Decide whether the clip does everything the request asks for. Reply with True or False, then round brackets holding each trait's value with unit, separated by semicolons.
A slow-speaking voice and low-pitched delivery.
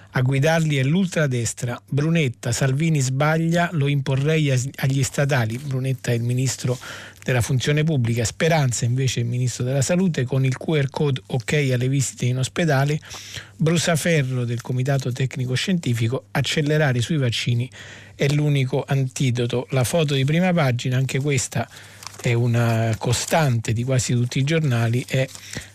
False (145 wpm; 130 Hz)